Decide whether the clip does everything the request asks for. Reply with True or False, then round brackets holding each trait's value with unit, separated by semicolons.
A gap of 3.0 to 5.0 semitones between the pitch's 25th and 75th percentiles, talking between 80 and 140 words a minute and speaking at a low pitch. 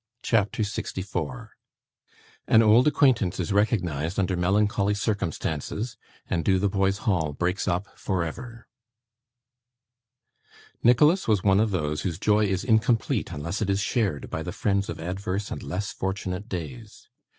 True (3.3 semitones; 135 wpm; 100 Hz)